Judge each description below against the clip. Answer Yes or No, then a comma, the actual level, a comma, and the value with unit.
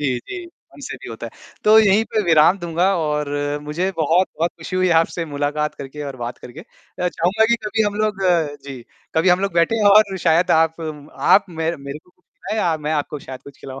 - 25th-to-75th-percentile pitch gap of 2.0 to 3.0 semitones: No, average, 4.3 semitones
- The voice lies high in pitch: No, medium, 165 Hz